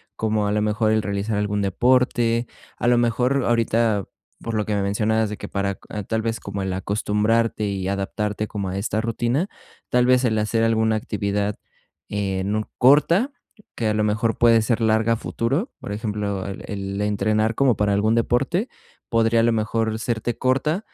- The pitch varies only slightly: Yes, narrow, 2.1 semitones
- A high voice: No, low, 110 Hz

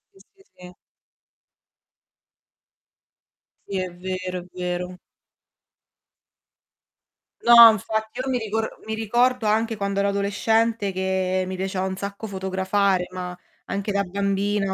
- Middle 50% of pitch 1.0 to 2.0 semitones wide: No, average, 2.7 semitones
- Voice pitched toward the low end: No, high, 200 Hz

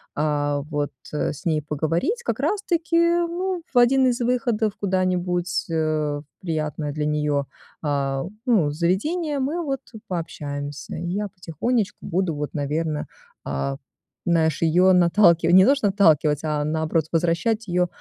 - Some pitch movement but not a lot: No, wide, 6.8 semitones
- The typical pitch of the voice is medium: Yes, medium, 170 Hz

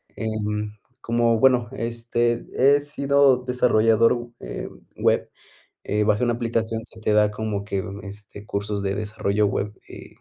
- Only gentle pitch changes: Yes, narrow, 2.2 semitones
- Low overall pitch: Yes, low, 110 Hz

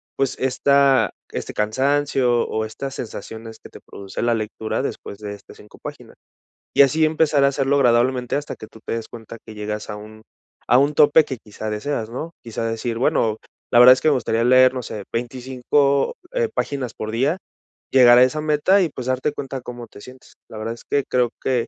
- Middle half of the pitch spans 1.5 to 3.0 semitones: No, average, 3.7 semitones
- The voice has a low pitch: Yes, low, 125 Hz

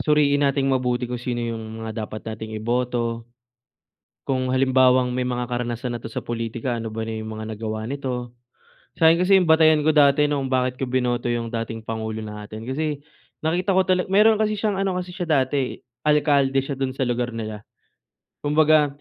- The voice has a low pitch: Yes, low, 130 Hz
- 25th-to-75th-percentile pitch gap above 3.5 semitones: Yes, average, 4.3 semitones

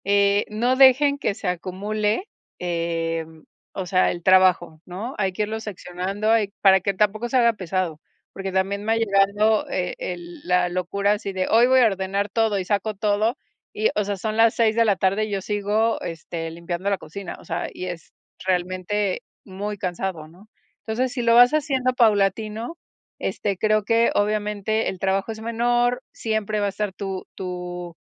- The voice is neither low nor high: No, high, 200 Hz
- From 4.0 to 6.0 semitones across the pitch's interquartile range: No, average, 3.1 semitones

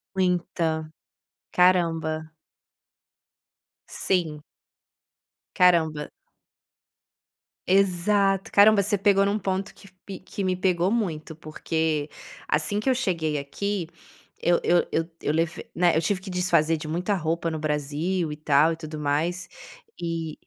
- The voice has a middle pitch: Yes, medium, 170 Hz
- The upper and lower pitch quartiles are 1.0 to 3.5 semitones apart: Yes, average, 3.2 semitones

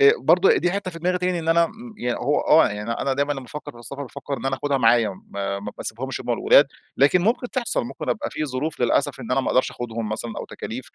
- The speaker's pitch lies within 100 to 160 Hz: Yes, medium, 140 Hz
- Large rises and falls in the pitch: Yes, wide, 6.6 semitones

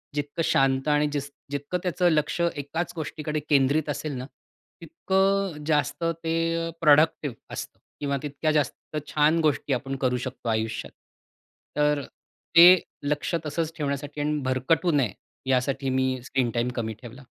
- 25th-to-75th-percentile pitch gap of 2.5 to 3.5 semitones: Yes, average, 3.2 semitones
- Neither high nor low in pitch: Yes, medium, 150 Hz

